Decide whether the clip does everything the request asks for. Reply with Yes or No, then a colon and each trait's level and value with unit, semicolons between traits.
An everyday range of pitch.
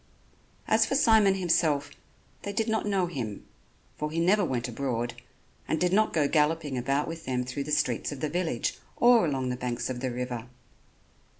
No: wide, 6.1 semitones